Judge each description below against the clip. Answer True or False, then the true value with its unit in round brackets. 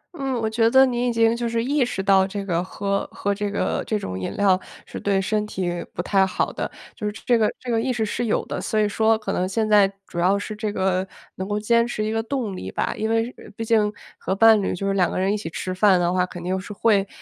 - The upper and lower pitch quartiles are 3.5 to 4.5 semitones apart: False (2.9 semitones)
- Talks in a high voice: True (210 Hz)